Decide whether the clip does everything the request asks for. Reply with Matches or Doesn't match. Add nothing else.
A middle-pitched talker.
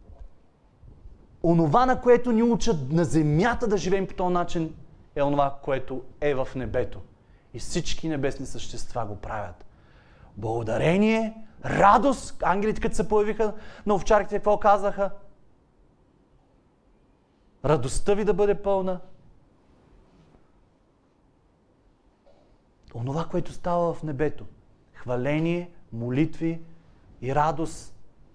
Matches